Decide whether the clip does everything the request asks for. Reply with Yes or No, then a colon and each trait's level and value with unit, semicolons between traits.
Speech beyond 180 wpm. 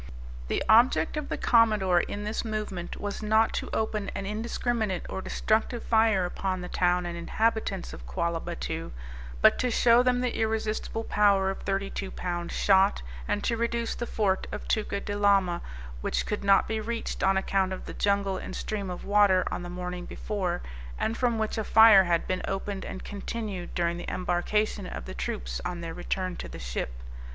Yes: average, 190 wpm